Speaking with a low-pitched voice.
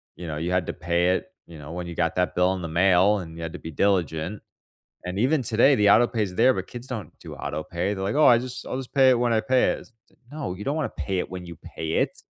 Yes: very low, 95 Hz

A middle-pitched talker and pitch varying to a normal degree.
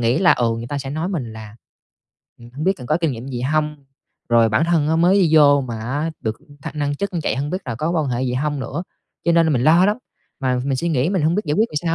Yes: medium, 145 Hz; average, 4.8 semitones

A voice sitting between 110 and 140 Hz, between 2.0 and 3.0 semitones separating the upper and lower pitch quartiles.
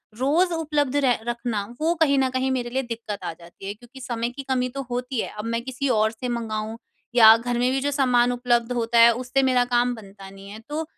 No: high, 245 Hz; narrow, 2.6 semitones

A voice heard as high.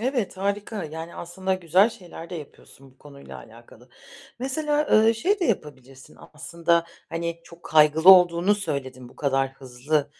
No: medium, 170 Hz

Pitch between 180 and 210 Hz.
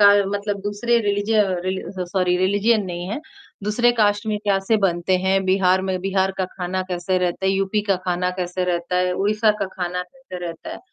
Yes: high, 190 Hz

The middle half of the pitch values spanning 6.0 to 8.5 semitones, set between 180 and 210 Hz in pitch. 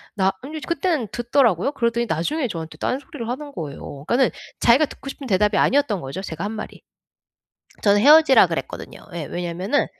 No: wide, 7.2 semitones; high, 235 Hz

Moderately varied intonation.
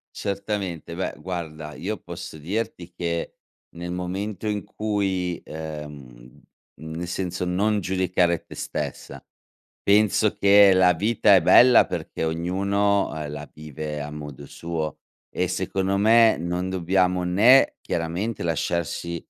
Yes: average, 3.3 semitones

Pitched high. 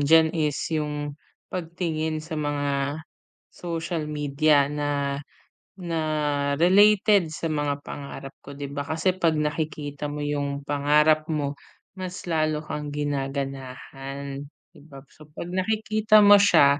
No: medium, 150 Hz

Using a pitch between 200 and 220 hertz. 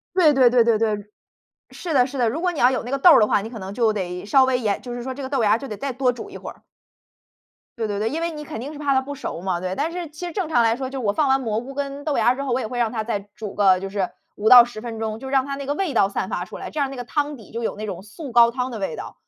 No: high, 245 Hz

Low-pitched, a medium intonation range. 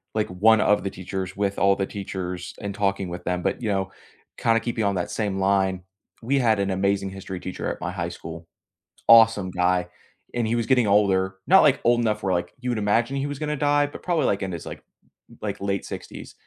Yes: low, 100 Hz; average, 3.4 semitones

